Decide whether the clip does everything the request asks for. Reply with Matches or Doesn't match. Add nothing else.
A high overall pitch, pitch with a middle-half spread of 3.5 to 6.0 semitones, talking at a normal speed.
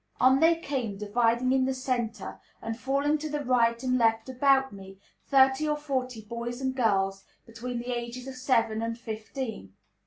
Doesn't match